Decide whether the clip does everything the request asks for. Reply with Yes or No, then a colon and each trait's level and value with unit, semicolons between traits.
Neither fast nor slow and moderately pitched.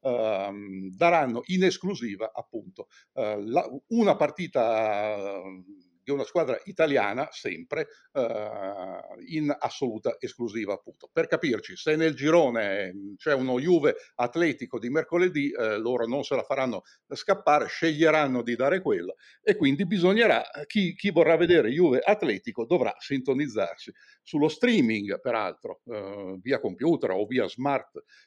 Yes: average, 130 wpm; medium, 160 Hz